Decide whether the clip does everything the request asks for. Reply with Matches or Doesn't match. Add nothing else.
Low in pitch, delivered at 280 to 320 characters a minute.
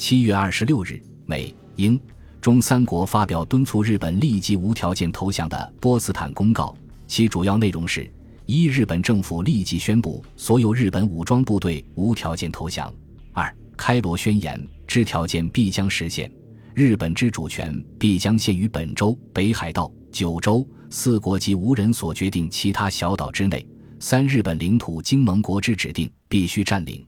Doesn't match